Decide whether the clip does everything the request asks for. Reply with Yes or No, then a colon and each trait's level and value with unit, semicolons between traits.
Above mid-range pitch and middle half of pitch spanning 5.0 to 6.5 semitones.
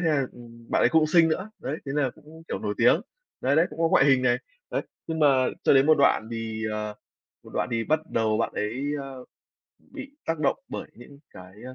No: low, 135 Hz; average, 5.3 semitones